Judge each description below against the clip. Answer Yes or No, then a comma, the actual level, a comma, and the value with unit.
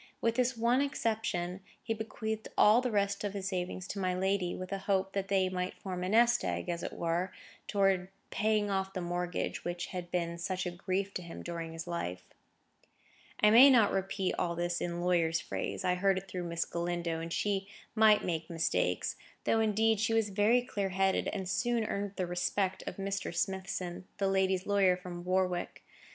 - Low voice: No, high, 190 Hz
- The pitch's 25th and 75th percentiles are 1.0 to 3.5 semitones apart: Yes, narrow, 2.6 semitones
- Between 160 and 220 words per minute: Yes, average, 195 wpm